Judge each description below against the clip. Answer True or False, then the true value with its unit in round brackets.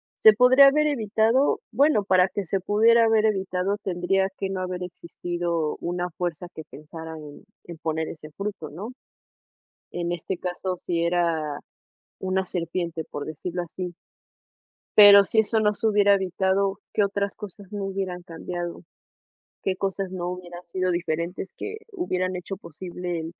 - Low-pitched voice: False (185 Hz)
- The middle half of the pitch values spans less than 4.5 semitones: True (2.7 semitones)